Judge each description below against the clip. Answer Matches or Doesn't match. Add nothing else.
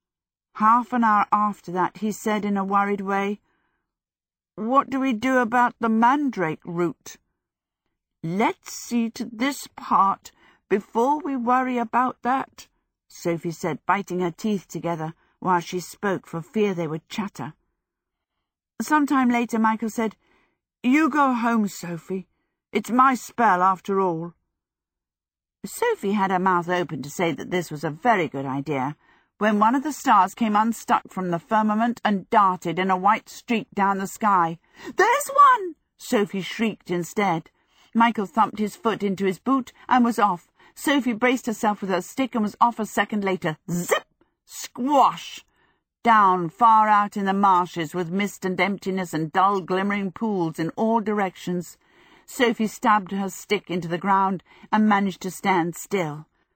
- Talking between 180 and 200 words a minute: Doesn't match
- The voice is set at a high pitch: Matches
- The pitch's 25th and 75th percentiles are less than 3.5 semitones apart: Doesn't match